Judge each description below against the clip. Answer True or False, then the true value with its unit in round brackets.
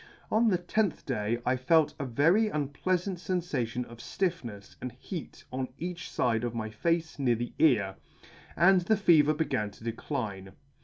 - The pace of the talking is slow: False (160 wpm)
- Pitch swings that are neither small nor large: False (7.0 semitones)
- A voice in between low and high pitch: True (145 Hz)